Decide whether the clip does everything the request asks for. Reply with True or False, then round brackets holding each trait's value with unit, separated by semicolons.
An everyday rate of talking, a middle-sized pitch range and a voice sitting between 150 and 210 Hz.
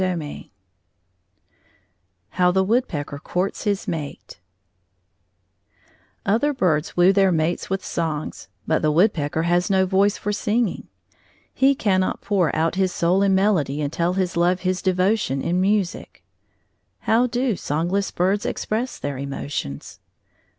False (130 wpm; 3.6 semitones; 185 Hz)